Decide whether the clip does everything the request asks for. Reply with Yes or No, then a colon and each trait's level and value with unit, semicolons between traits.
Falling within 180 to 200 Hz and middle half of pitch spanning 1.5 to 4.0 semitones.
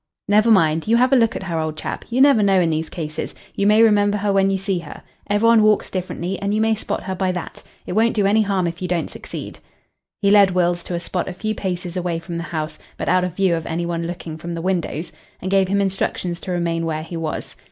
Yes: medium, 185 Hz; average, 3.2 semitones